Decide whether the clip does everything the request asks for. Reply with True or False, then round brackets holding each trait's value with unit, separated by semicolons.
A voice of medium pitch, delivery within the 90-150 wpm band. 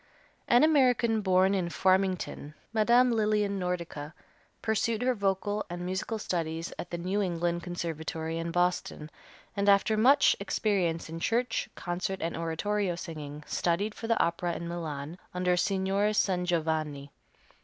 True (180 Hz; 135 wpm)